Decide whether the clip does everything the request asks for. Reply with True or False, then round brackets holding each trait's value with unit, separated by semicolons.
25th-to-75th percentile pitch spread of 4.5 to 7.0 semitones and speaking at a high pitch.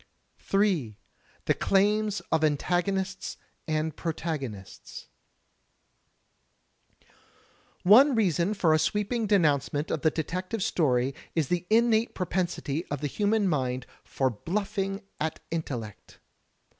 False (5.4 semitones; 175 Hz)